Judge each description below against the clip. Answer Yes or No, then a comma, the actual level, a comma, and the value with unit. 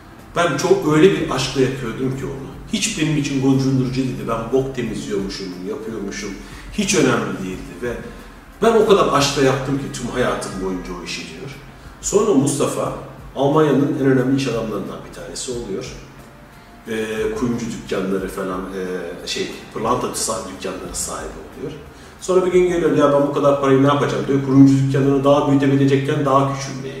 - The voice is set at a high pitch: No, low, 135 Hz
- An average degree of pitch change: Yes, average, 4.5 semitones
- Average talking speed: No, fast, 155 wpm